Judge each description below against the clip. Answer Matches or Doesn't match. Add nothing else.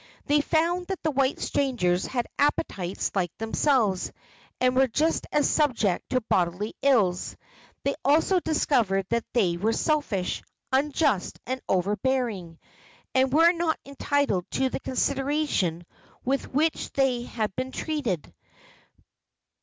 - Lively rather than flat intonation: Matches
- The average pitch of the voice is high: Matches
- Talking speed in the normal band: Doesn't match